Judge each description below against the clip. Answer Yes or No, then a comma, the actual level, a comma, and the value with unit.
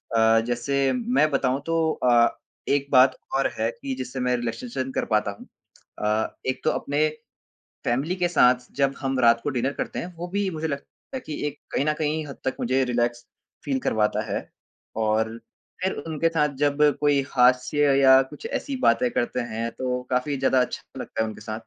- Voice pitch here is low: Yes, low, 130 Hz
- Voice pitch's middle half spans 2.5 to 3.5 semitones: No, average, 3.9 semitones